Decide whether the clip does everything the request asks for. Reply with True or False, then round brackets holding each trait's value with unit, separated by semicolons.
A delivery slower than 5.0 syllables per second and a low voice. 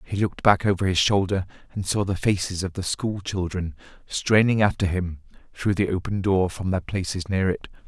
False (5.2 syllables/s; 95 Hz)